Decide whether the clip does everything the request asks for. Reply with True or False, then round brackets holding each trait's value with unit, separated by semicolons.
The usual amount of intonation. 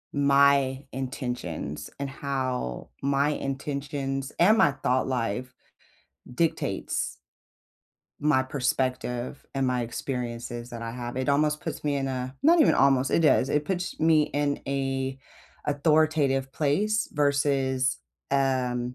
False (2.1 semitones)